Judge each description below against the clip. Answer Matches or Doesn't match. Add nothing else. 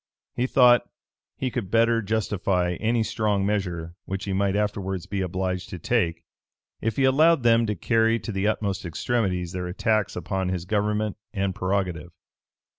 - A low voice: Matches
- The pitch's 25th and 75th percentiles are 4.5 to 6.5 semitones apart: Doesn't match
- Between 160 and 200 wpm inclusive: Matches